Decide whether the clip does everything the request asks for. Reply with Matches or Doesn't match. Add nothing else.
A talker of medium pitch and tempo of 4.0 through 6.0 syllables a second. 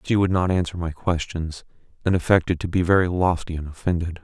Doesn't match